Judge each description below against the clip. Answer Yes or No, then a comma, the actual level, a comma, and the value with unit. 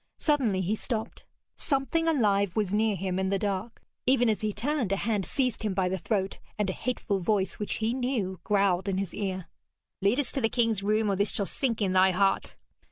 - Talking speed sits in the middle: No, fast, 215 wpm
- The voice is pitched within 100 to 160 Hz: No, high, 205 Hz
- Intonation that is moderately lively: Yes, average, 3.3 semitones